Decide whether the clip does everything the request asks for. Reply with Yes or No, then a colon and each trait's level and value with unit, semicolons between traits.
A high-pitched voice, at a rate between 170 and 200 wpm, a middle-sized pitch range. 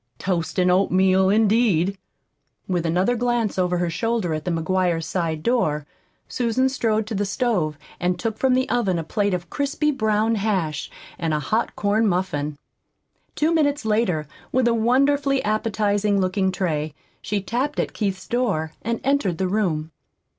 No: high, 200 Hz; average, 160 wpm; average, 4.7 semitones